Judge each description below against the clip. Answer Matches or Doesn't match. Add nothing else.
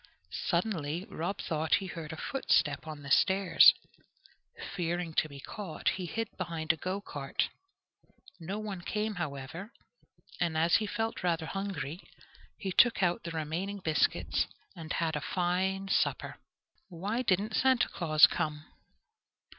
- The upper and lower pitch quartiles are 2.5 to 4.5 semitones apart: Matches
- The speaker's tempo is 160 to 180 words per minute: Doesn't match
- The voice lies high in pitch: Doesn't match